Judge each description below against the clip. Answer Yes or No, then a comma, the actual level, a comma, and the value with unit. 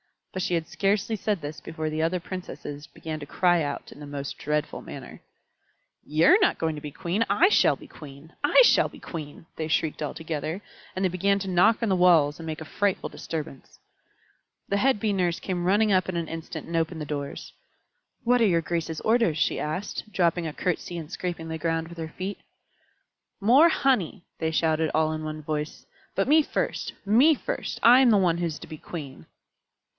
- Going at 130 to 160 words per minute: No, fast, 205 wpm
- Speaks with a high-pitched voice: No, medium, 170 Hz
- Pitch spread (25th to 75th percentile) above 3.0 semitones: Yes, average, 4.0 semitones